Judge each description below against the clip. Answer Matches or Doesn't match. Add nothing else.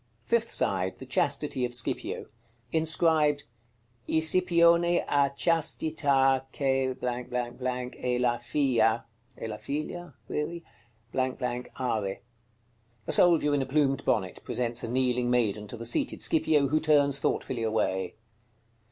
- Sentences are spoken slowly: Matches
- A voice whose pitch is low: Matches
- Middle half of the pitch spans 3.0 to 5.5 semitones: Matches